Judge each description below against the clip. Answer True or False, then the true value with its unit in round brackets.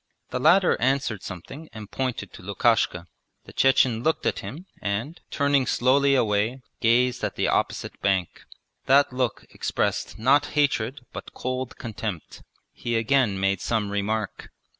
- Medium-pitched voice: False (120 Hz)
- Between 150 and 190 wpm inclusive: False (140 wpm)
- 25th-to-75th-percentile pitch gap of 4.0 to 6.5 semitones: True (4.4 semitones)